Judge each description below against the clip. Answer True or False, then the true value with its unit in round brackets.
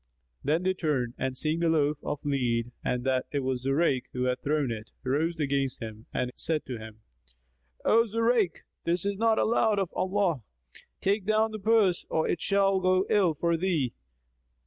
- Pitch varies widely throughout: True (6.8 semitones)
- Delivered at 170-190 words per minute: True (180 wpm)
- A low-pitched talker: False (160 Hz)